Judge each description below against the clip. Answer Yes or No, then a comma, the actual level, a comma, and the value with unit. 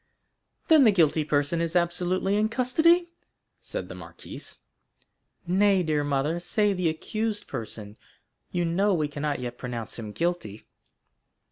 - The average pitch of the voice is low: No, medium, 175 Hz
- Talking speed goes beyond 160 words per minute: No, slow, 135 wpm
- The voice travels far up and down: Yes, wide, 6.0 semitones